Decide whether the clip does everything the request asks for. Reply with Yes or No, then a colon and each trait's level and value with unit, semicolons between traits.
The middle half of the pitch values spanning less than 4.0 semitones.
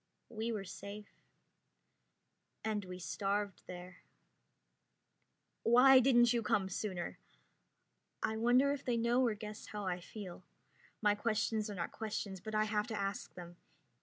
Yes: average, 2.9 semitones